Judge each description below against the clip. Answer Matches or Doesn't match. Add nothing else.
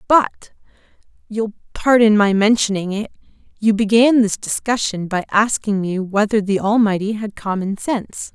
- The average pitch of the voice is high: Matches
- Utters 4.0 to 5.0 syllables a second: Matches